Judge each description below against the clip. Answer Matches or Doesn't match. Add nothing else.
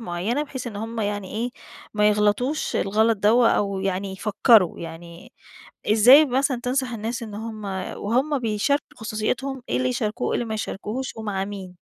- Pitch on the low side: Doesn't match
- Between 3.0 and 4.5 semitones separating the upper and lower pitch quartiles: Matches